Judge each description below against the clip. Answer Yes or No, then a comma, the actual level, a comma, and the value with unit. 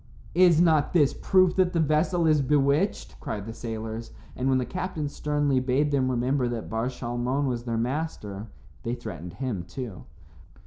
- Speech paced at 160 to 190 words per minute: Yes, average, 170 wpm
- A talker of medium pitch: No, low, 130 Hz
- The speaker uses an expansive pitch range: No, average, 4.4 semitones